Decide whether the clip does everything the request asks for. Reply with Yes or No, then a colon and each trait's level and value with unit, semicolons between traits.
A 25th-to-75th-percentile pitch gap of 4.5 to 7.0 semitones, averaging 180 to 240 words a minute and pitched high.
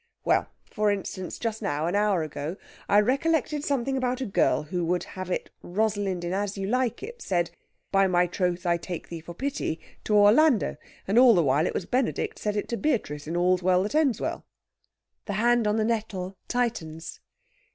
Yes: average, 5.1 semitones; average, 195 wpm; high, 200 Hz